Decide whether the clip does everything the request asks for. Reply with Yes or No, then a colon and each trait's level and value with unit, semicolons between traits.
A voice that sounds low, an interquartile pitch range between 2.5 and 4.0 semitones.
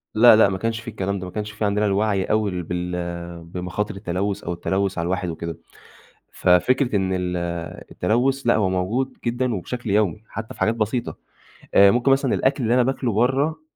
No: low, 105 Hz; average, 4.6 semitones